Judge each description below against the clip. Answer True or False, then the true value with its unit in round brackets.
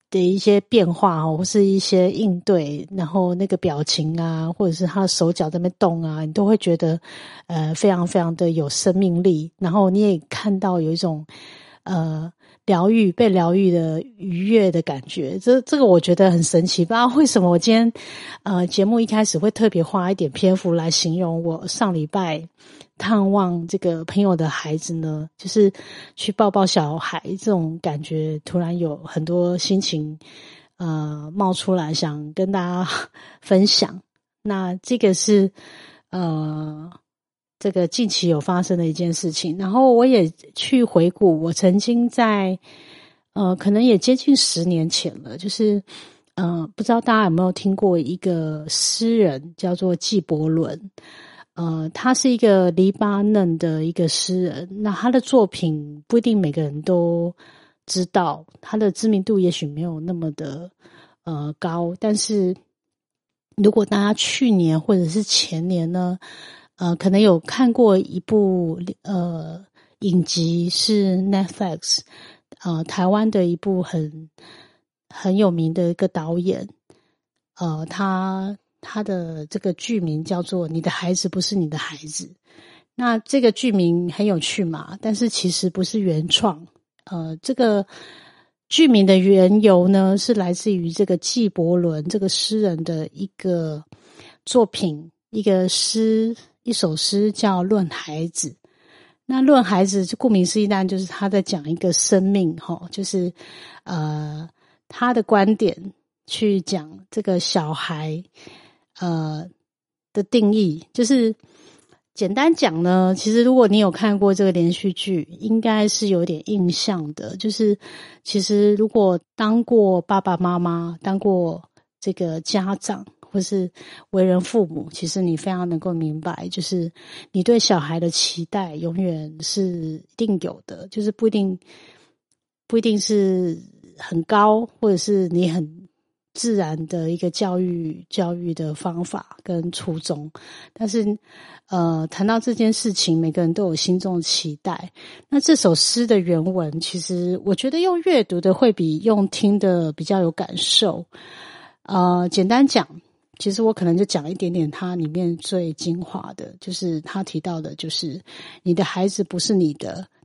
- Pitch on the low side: False (185 Hz)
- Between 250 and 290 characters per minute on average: False (220 characters per minute)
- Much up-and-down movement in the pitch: False (3.5 semitones)